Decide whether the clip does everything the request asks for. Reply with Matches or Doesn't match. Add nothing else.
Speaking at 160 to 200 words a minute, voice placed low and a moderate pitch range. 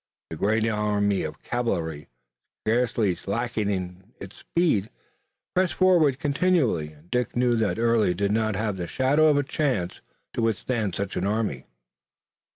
Doesn't match